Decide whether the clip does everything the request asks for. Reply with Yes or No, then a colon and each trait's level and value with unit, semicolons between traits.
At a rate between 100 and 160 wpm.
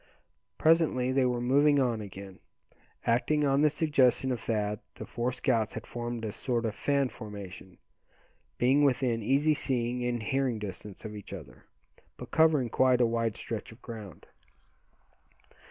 Yes: average, 155 wpm